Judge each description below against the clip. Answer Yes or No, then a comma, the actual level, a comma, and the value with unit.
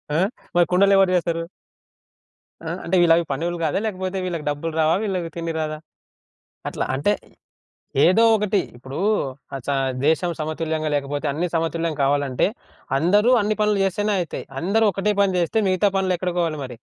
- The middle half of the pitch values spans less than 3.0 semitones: No, average, 3.6 semitones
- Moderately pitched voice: Yes, medium, 170 Hz